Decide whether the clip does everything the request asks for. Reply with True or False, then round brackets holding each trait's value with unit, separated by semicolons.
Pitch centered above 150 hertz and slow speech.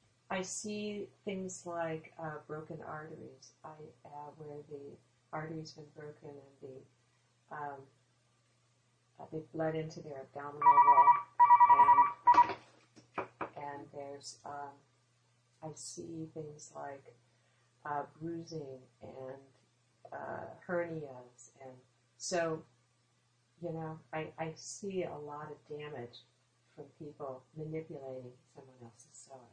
False (145 Hz; 110 wpm)